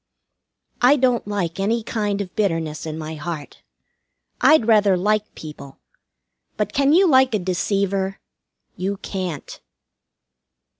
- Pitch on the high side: Yes, high, 200 Hz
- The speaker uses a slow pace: Yes, slow, 120 wpm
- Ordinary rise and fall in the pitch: Yes, average, 3.9 semitones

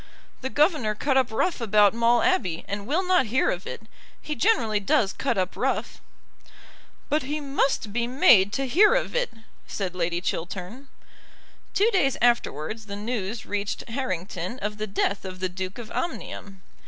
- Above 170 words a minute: No, average, 165 wpm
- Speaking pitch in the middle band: No, high, 220 Hz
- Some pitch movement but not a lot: No, wide, 5.9 semitones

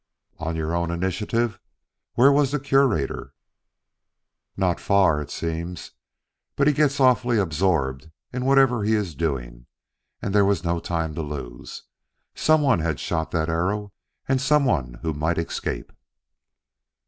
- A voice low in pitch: Yes, very low, 90 Hz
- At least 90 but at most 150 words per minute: Yes, average, 140 wpm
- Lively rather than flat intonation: Yes, wide, 7.4 semitones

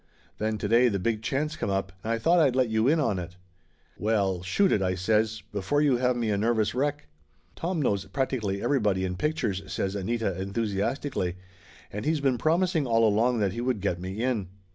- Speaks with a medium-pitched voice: No, low, 110 Hz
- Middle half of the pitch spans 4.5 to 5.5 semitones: Yes, average, 5.0 semitones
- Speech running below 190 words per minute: No, fast, 205 wpm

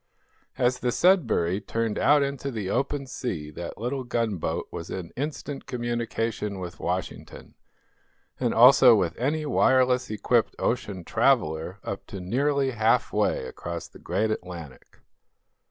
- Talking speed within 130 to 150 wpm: Yes, slow, 135 wpm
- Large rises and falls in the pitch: Yes, wide, 6.0 semitones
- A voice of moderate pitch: No, low, 115 Hz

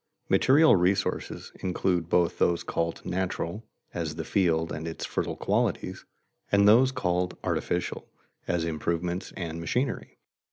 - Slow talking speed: Yes, slow, 130 wpm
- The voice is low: Yes, very low, 90 Hz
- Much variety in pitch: No, average, 2.8 semitones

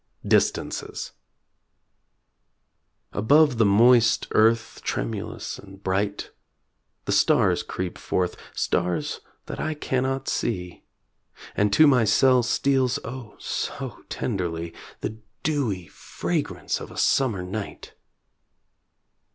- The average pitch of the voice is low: Yes, low, 110 Hz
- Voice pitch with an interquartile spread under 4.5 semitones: No, average, 5.0 semitones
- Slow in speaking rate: Yes, slow, 100 wpm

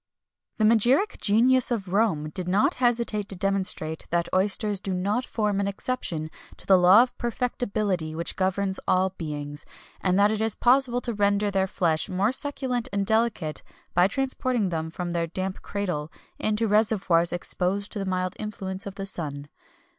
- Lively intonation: No, average, 3.6 semitones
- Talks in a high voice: Yes, high, 195 Hz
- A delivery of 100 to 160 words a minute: No, average, 170 wpm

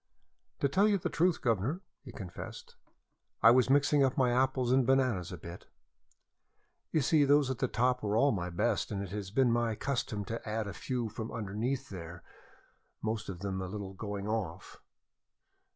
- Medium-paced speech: Yes, average, 185 wpm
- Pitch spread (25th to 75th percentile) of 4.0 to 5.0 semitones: Yes, average, 4.6 semitones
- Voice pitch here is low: Yes, low, 115 Hz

